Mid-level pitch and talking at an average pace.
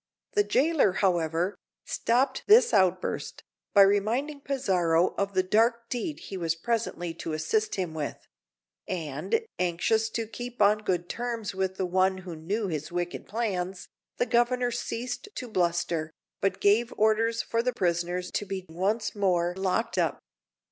No: high, 200 Hz; average, 150 wpm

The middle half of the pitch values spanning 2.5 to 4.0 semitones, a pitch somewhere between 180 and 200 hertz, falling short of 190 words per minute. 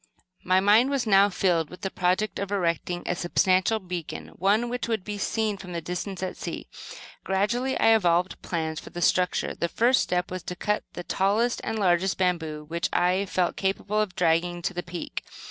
No: average, 2.9 semitones; medium, 185 Hz; average, 195 wpm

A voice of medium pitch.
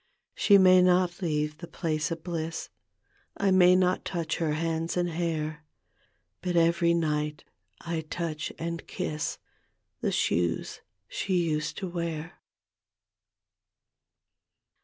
Yes: medium, 170 Hz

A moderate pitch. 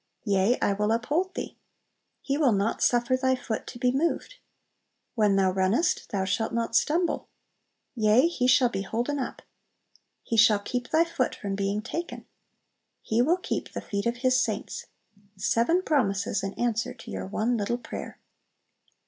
No: high, 235 Hz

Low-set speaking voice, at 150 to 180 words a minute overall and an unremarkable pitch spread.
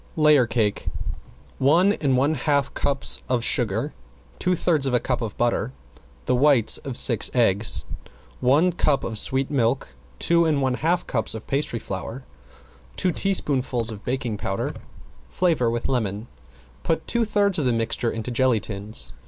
Yes: low, 130 Hz; average, 160 wpm; average, 4.7 semitones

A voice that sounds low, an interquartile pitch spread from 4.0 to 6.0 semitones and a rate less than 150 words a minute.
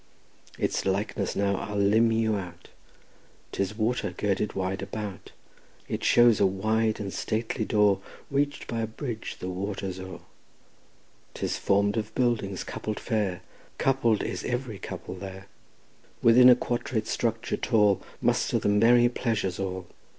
No: low, 105 Hz; average, 2.9 semitones; average, 140 wpm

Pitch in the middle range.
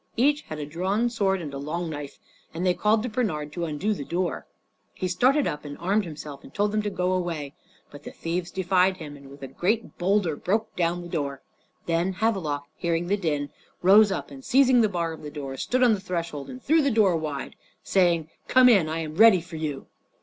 Yes: medium, 175 Hz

